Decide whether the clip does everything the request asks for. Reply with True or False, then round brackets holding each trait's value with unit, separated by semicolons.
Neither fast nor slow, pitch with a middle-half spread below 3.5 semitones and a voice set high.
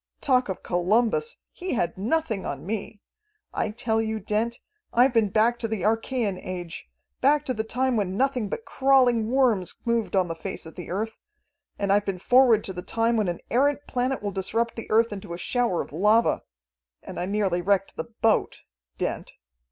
False (190 wpm; 4.0 semitones; 220 Hz)